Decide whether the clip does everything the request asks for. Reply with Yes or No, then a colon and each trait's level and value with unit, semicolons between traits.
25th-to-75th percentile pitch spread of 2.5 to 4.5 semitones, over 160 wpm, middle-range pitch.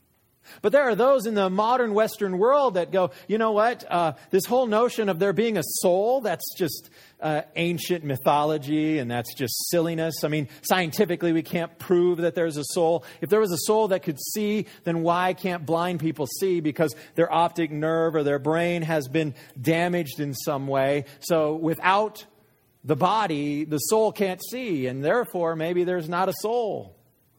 Yes: average, 4.0 semitones; average, 185 wpm; medium, 170 Hz